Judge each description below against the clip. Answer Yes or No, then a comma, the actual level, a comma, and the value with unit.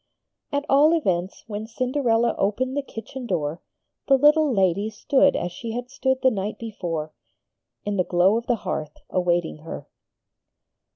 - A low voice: No, high, 225 Hz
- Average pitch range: No, wide, 6.3 semitones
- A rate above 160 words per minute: No, average, 155 wpm